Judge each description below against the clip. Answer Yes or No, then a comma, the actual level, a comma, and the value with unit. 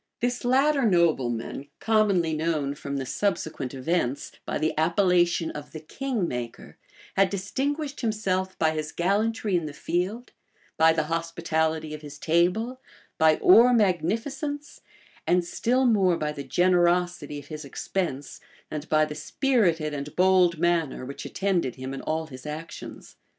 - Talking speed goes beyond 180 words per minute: No, average, 145 wpm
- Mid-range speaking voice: Yes, medium, 170 Hz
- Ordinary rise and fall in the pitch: Yes, average, 4.8 semitones